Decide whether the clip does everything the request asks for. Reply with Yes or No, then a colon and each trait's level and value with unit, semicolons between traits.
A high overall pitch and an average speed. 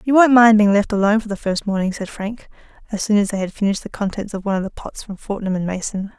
No: high, 205 Hz; fast, 280 wpm